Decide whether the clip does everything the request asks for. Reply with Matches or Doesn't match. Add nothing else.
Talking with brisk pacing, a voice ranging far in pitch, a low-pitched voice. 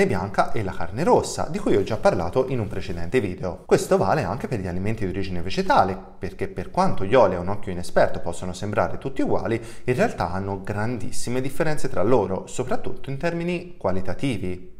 Matches